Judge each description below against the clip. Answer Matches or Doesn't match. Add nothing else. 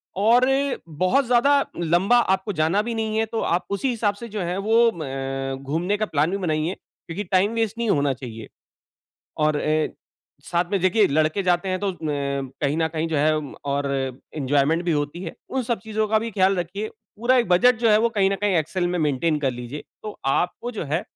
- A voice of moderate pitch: Matches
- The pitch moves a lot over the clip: Matches